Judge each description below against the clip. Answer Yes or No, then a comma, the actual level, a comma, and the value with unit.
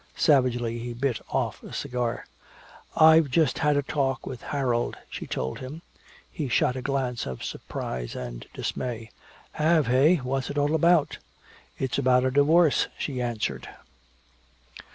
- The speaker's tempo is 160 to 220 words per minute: No, average, 145 wpm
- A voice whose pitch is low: Yes, low, 130 Hz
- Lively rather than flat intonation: No, average, 3.3 semitones